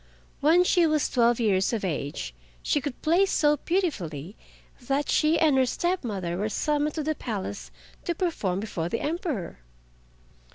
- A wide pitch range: Yes, wide, 8.5 semitones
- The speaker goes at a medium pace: Yes, average, 160 wpm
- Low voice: No, very high, 265 Hz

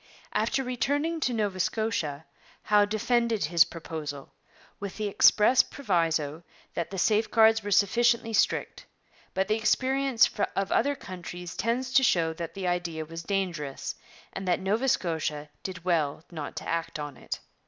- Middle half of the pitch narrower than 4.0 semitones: No, wide, 5.5 semitones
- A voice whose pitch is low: No, high, 195 Hz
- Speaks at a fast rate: No, average, 150 wpm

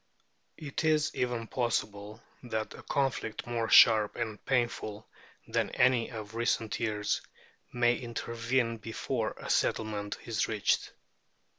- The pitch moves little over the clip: Yes, narrow, 2.0 semitones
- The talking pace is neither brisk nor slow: No, slow, 120 wpm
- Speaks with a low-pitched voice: Yes, low, 115 Hz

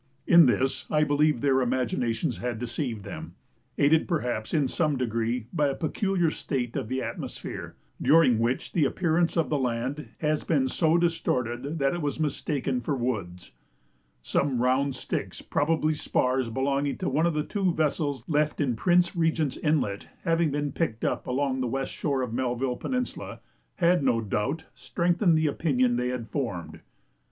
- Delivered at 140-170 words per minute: Yes, average, 165 wpm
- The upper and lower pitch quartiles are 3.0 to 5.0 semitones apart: Yes, average, 4.1 semitones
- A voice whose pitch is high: No, medium, 140 Hz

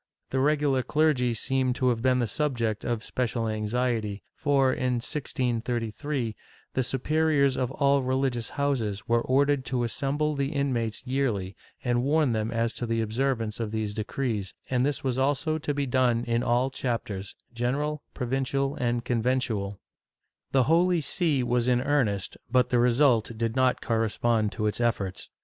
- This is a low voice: Yes, low, 125 Hz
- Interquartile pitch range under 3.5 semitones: Yes, average, 3.0 semitones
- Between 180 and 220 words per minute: No, average, 160 wpm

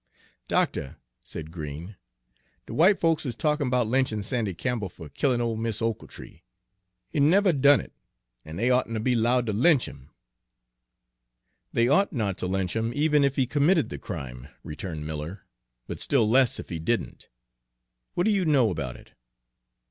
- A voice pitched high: No, low, 115 Hz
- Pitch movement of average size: No, wide, 7.3 semitones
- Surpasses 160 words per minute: Yes, average, 170 wpm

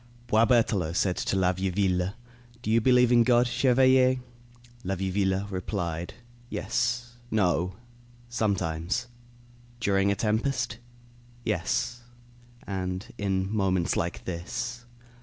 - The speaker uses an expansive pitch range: No, average, 4.4 semitones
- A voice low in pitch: Yes, low, 100 Hz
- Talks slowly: Yes, slow, 100 wpm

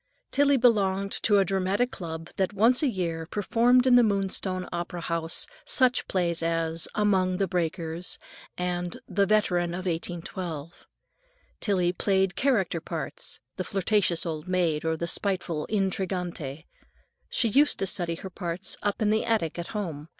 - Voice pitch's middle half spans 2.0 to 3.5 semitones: Yes, average, 3.2 semitones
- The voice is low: No, medium, 185 Hz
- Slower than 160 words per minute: Yes, average, 150 wpm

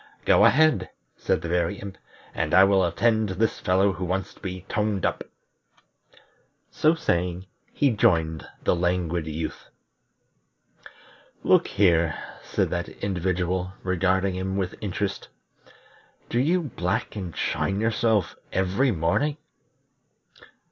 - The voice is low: Yes, very low, 95 Hz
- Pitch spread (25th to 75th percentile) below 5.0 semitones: Yes, average, 2.9 semitones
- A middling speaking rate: No, slow, 125 wpm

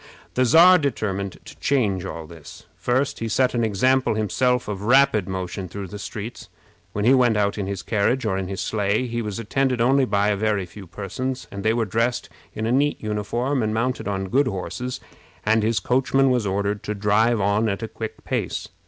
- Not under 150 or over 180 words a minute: No, fast, 205 wpm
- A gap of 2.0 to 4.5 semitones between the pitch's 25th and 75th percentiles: Yes, average, 3.9 semitones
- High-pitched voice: No, low, 110 Hz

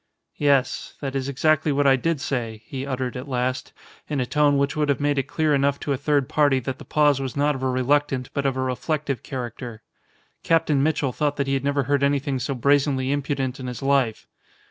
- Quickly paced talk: Yes, fast, 220 wpm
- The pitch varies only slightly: Yes, narrow, 1.8 semitones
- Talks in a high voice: No, medium, 140 Hz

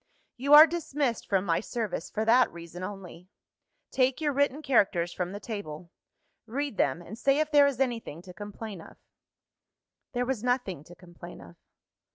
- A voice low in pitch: No, high, 220 Hz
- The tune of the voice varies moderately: No, wide, 7.1 semitones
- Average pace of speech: Yes, average, 170 wpm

